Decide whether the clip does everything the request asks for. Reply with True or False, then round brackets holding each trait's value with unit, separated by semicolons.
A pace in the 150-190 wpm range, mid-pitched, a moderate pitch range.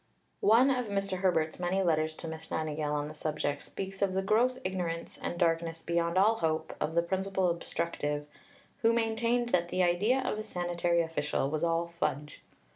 True (180 wpm; 170 Hz; 3.4 semitones)